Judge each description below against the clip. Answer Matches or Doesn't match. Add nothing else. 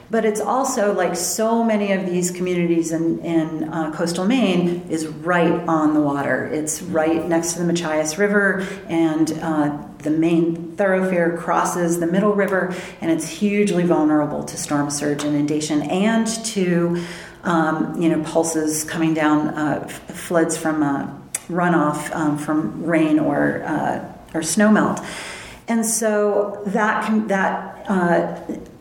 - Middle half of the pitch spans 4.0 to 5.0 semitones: Doesn't match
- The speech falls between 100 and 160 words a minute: Matches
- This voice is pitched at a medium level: Matches